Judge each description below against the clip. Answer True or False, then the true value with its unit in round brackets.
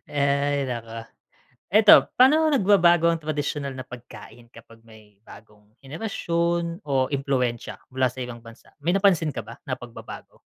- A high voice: False (140 Hz)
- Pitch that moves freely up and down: True (6.0 semitones)